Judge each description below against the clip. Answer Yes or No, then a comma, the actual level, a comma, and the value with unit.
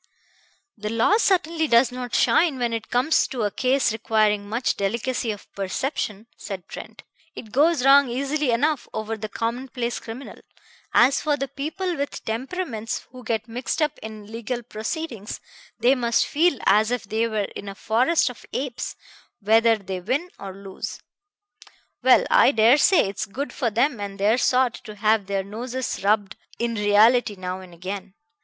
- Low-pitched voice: No, high, 230 Hz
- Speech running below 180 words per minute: Yes, average, 165 wpm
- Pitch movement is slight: No, average, 4.0 semitones